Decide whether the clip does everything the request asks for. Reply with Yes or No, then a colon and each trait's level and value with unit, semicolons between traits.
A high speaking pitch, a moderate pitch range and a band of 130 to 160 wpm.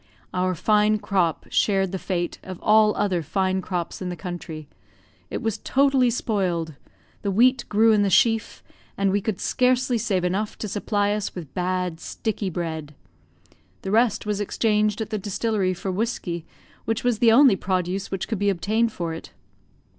No: high, 200 Hz; average, 3.3 semitones; average, 170 wpm